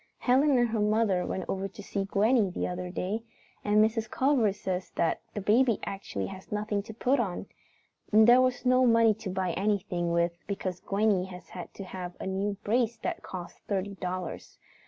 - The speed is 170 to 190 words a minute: Yes, average, 185 wpm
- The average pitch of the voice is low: No, high, 200 Hz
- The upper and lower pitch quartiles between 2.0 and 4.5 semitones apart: Yes, average, 3.3 semitones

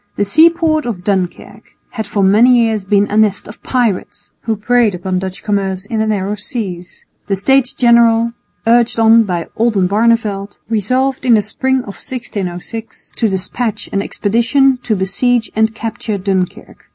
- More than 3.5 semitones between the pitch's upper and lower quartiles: No, average, 3.2 semitones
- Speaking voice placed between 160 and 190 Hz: No, high, 220 Hz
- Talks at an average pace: Yes, average, 155 wpm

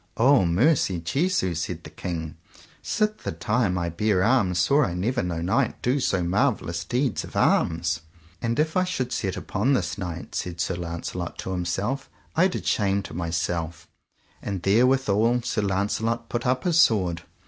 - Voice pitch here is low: Yes, low, 100 Hz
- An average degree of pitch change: No, wide, 6.4 semitones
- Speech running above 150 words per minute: Yes, average, 170 wpm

